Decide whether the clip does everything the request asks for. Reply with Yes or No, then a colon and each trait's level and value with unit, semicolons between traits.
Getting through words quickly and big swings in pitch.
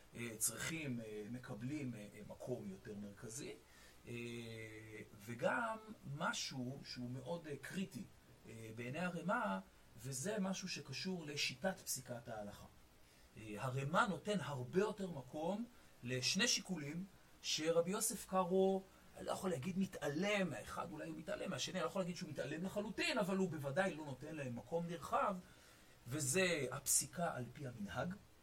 No: average, 120 wpm; wide, 8.7 semitones